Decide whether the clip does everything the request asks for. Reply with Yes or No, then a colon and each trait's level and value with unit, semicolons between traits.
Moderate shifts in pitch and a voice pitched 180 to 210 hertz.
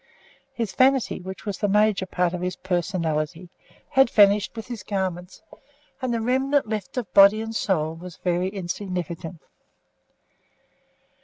Yes: average, 3.8 semitones; high, 190 Hz